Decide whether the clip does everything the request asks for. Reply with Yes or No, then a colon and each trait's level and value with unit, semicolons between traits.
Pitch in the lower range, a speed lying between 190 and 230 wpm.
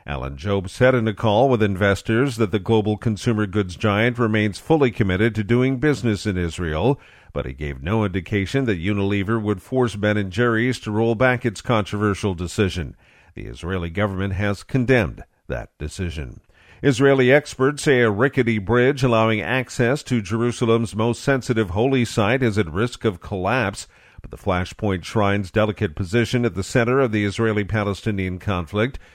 No: low, 110 Hz; average, 165 wpm